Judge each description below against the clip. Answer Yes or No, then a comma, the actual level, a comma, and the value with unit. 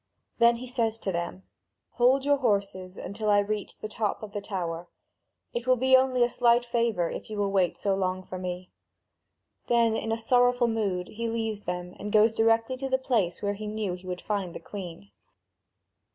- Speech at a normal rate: Yes, average, 195 wpm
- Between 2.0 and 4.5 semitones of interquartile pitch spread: Yes, average, 4.0 semitones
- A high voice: Yes, high, 215 Hz